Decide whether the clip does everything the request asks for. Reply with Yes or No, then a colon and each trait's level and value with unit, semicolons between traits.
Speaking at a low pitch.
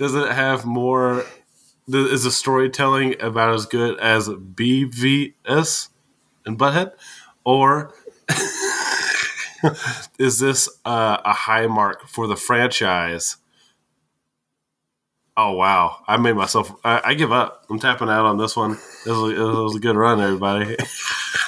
Yes: low, 125 Hz